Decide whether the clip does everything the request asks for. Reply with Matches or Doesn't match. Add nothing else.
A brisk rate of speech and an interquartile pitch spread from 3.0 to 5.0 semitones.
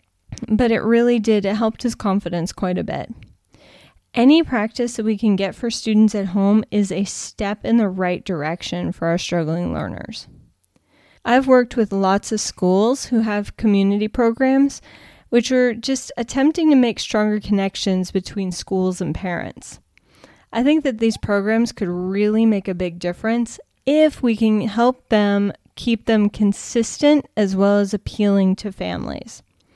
Doesn't match